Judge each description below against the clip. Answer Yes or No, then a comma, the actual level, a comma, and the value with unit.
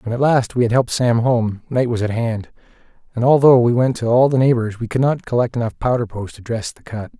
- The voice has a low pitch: Yes, low, 120 Hz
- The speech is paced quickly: Yes, fast, 260 wpm